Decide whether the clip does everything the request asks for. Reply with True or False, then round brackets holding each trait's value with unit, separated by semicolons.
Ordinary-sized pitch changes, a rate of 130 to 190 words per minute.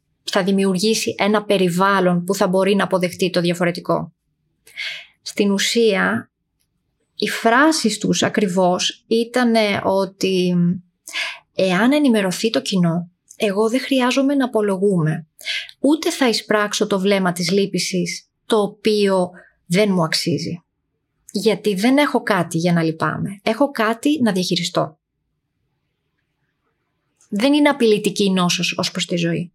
False (3.9 semitones; 120 wpm)